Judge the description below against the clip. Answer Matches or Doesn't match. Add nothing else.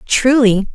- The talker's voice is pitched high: Matches